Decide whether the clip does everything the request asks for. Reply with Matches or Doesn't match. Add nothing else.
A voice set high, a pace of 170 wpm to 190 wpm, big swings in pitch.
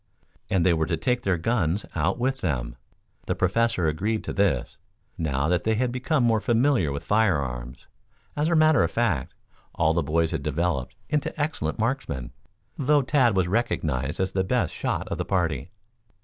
Doesn't match